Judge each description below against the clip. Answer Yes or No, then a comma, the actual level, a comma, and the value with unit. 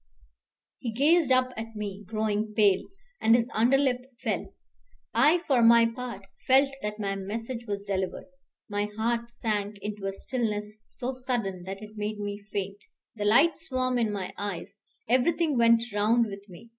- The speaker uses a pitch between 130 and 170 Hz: No, high, 220 Hz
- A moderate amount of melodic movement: Yes, average, 3.3 semitones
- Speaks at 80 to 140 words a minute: No, average, 160 wpm